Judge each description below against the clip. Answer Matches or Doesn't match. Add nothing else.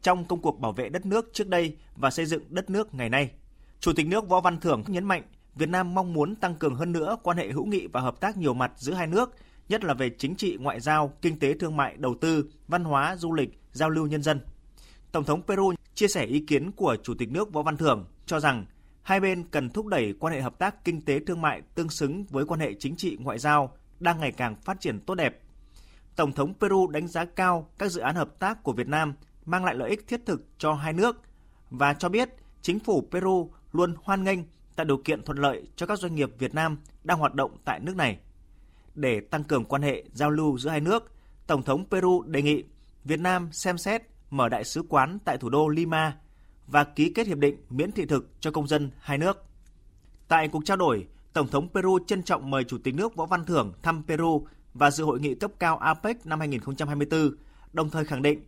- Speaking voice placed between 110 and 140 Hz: Doesn't match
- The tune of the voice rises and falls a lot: Doesn't match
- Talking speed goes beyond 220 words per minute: Matches